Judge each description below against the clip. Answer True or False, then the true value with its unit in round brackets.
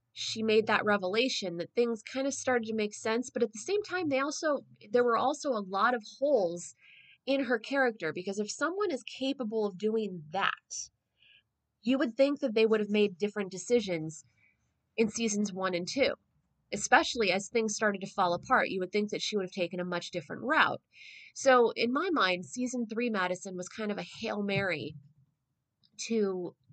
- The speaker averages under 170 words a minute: False (190 wpm)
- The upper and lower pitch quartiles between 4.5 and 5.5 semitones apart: True (5.1 semitones)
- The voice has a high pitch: True (215 Hz)